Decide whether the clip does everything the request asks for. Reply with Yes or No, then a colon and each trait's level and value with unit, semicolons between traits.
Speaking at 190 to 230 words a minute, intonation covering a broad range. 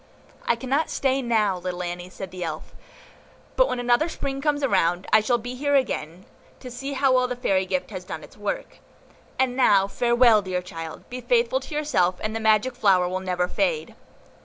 Yes: average, 195 wpm; wide, 6.2 semitones